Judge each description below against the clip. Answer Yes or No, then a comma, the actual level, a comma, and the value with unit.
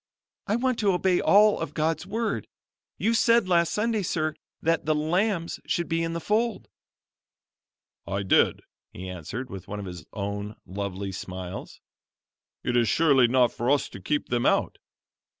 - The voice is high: No, medium, 155 Hz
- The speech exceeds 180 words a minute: No, average, 165 wpm